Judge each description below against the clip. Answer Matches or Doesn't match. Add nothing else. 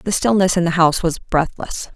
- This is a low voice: Doesn't match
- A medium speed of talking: Doesn't match